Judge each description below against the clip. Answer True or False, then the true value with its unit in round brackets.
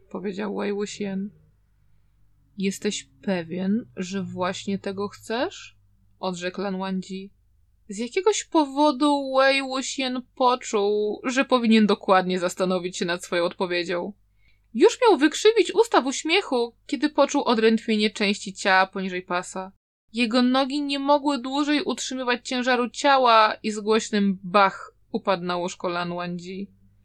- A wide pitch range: True (5.9 semitones)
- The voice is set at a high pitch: True (205 Hz)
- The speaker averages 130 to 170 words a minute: False (120 wpm)